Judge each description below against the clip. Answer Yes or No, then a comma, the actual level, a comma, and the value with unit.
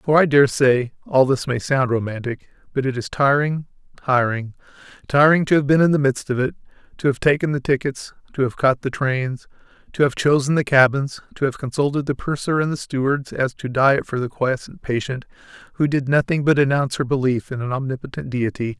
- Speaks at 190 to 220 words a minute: Yes, average, 200 wpm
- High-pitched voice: No, low, 135 Hz